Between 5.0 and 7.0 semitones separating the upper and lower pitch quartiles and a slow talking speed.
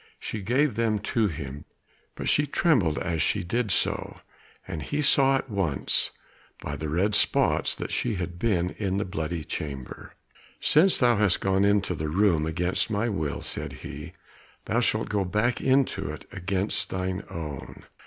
No: average, 5.3 semitones; average, 165 wpm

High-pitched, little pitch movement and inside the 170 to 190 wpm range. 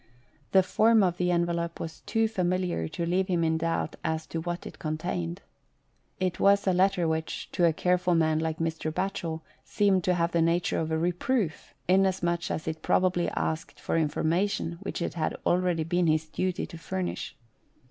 No: medium, 170 Hz; narrow, 2.3 semitones; average, 180 wpm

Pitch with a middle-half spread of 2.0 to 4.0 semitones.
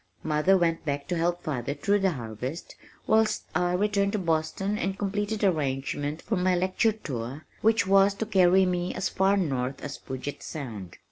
No: wide, 5.4 semitones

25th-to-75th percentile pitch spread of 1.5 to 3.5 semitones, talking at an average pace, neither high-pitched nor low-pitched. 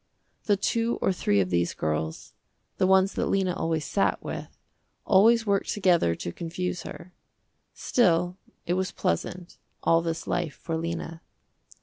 Yes: average, 2.8 semitones; average, 145 wpm; medium, 175 Hz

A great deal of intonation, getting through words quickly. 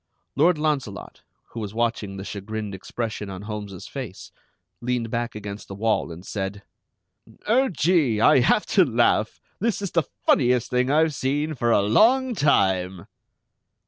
No: wide, 6.6 semitones; average, 150 wpm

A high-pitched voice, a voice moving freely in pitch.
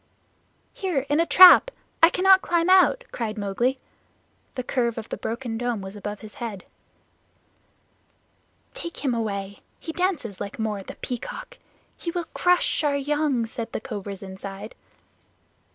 Yes: high, 245 Hz; wide, 8.0 semitones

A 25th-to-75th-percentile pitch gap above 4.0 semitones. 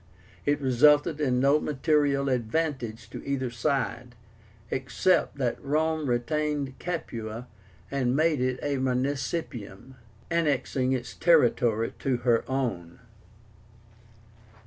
No: average, 3.3 semitones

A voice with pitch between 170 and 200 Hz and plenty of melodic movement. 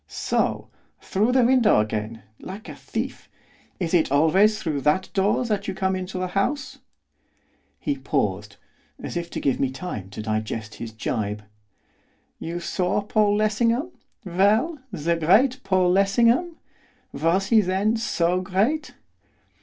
Yes: medium, 185 Hz; wide, 6.4 semitones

